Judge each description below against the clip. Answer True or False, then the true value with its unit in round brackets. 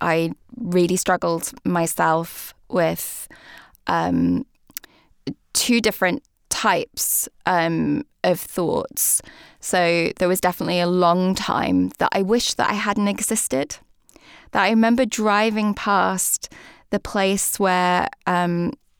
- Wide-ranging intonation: False (3.2 semitones)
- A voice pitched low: False (185 Hz)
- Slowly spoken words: True (110 wpm)